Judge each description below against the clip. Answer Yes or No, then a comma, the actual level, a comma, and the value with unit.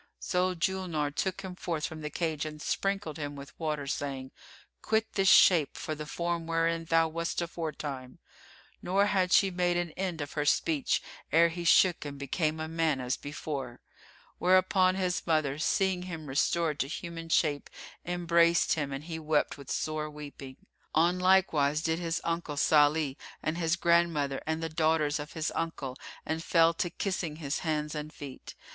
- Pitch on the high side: No, medium, 160 Hz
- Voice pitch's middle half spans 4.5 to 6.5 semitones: No, narrow, 2.6 semitones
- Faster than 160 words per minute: Yes, average, 175 wpm